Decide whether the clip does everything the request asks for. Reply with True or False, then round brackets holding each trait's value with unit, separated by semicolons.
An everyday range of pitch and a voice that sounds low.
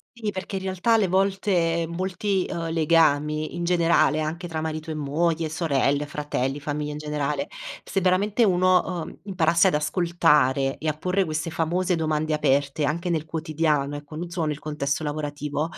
False (3.0 semitones; 160 Hz)